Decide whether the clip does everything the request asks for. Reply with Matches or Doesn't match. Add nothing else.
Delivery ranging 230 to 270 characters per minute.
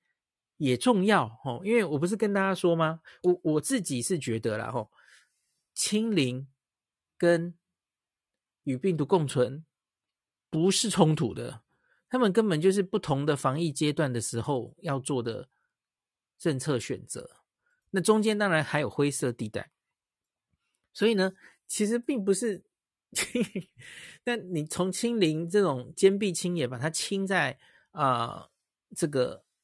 Doesn't match